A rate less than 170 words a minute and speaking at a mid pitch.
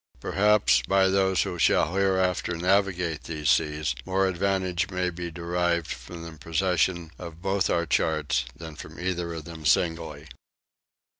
No: average, 145 wpm; very low, 85 Hz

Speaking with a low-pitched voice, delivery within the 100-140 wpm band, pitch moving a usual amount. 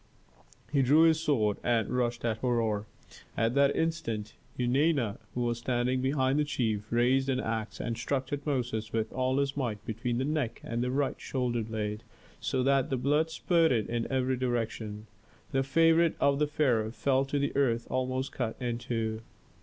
No: low, 125 Hz; average, 175 wpm; average, 3.3 semitones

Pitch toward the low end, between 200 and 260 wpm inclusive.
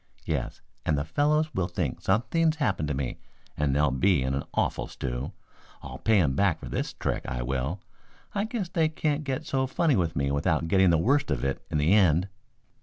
Yes: very low, 90 Hz; fast, 205 wpm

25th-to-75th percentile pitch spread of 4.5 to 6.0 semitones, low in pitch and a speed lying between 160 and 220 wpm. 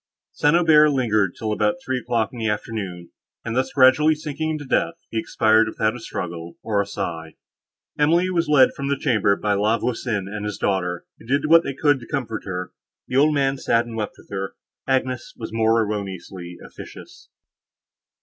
Yes: average, 5.2 semitones; low, 115 Hz; average, 190 wpm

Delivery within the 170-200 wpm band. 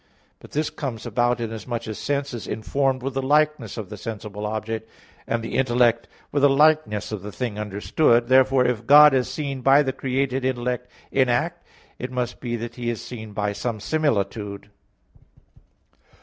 Yes: average, 175 wpm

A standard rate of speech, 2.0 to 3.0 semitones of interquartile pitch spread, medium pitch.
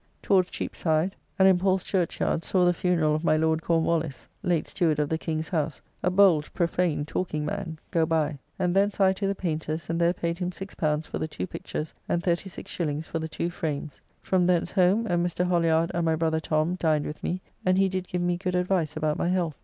No: fast, 215 wpm; narrow, 2.4 semitones; medium, 170 Hz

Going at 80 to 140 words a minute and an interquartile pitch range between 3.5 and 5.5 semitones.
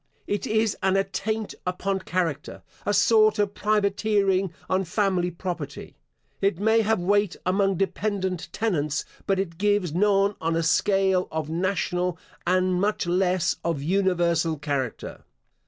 No: slow, 135 wpm; average, 2.8 semitones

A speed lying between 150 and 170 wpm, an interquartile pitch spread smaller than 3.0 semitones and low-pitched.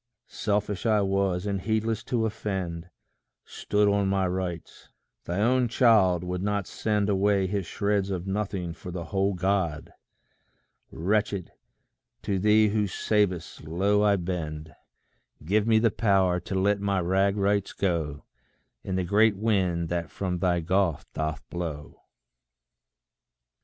No: slow, 135 wpm; narrow, 2.5 semitones; very low, 95 Hz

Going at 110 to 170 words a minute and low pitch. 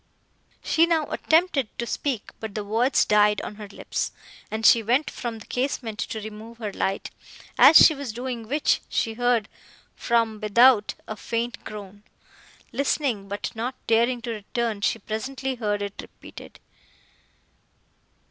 No: average, 150 wpm; high, 230 Hz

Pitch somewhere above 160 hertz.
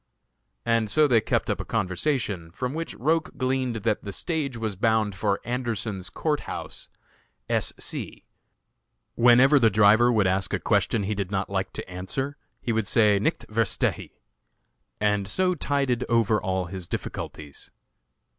No: low, 110 Hz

